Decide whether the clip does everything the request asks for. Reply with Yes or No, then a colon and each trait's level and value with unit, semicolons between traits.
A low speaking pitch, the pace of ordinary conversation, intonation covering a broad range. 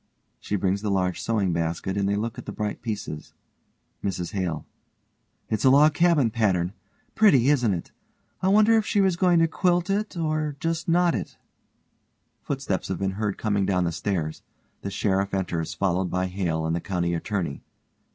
Yes: low, 100 Hz; average, 175 wpm; wide, 8.8 semitones